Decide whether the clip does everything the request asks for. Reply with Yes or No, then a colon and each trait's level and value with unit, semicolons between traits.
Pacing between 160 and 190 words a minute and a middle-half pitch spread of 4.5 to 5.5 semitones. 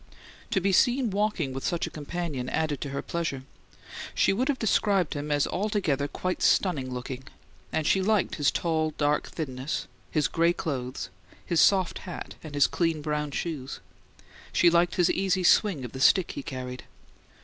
Yes: average, 170 wpm; average, 4.8 semitones